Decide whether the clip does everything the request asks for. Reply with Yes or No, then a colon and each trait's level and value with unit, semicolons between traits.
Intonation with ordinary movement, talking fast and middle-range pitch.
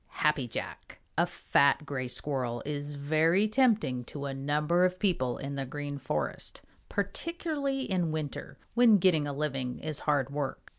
No: average, 5.0 semitones; average, 155 wpm; medium, 150 Hz